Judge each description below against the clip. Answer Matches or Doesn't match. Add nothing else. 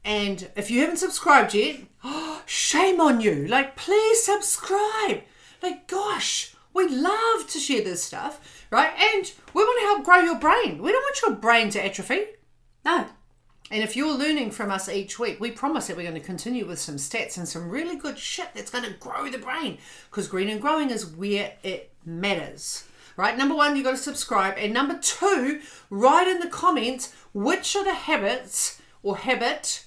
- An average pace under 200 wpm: Matches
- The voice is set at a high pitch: Matches